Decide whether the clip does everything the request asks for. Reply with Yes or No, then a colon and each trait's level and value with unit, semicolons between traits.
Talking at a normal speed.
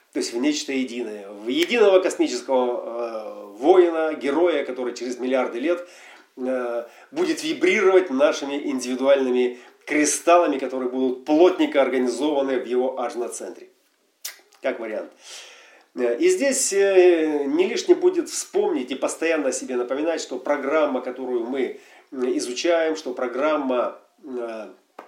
Yes: average, 120 wpm